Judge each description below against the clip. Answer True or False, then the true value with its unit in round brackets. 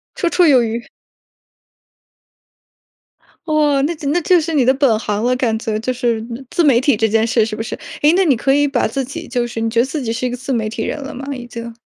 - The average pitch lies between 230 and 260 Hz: True (250 Hz)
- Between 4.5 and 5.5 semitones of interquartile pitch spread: False (4.1 semitones)